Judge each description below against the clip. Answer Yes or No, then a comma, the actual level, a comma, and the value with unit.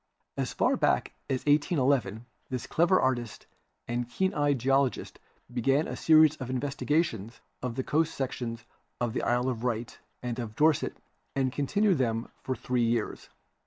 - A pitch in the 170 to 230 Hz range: No, low, 130 Hz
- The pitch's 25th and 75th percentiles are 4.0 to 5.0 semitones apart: No, average, 3.5 semitones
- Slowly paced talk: No, average, 160 wpm